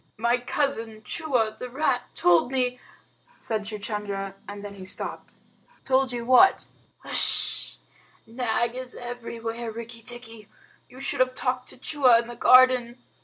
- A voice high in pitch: Yes, high, 240 Hz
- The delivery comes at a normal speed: Yes, average, 145 wpm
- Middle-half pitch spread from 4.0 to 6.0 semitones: No, narrow, 2.4 semitones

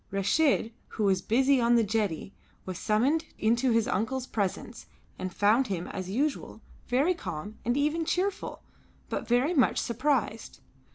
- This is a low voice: No, high, 235 Hz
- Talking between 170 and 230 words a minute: No, average, 150 wpm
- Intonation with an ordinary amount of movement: Yes, average, 4.8 semitones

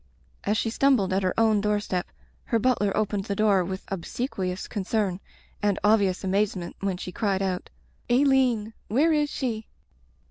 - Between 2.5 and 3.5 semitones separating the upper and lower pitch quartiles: Yes, average, 3.0 semitones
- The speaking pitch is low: No, high, 205 Hz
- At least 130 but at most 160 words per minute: No, average, 170 wpm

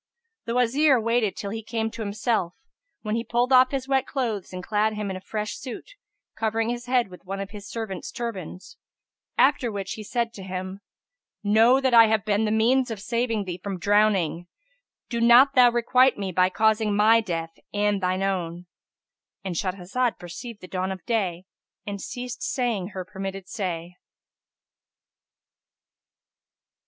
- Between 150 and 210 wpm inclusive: Yes, average, 165 wpm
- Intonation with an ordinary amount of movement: Yes, average, 3.7 semitones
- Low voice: No, high, 215 Hz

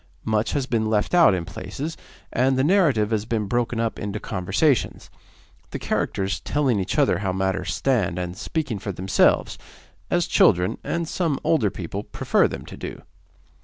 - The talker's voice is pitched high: No, low, 110 Hz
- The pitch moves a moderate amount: No, wide, 5.9 semitones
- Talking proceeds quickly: No, average, 165 wpm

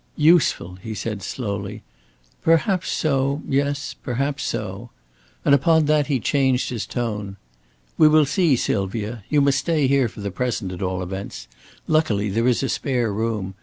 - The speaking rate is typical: Yes, average, 160 wpm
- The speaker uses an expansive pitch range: Yes, wide, 5.7 semitones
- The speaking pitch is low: Yes, low, 125 Hz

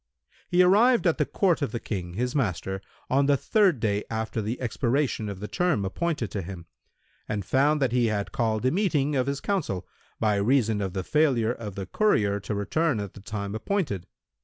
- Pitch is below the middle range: Yes, low, 115 Hz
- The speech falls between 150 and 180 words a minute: No, average, 200 wpm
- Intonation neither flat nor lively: No, wide, 6.6 semitones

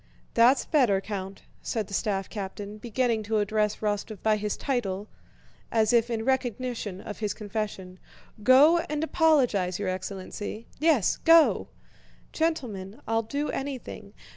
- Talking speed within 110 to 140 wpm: Yes, slow, 135 wpm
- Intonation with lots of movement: No, average, 4.1 semitones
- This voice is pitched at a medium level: No, high, 220 Hz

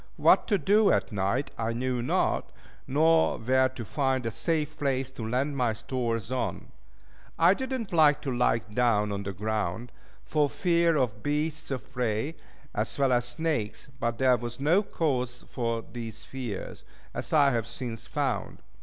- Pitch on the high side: No, low, 130 Hz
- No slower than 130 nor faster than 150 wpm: No, average, 170 wpm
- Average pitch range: Yes, average, 4.3 semitones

